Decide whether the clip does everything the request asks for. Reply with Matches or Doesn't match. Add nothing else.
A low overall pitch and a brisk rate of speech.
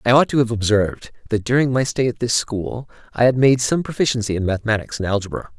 Matches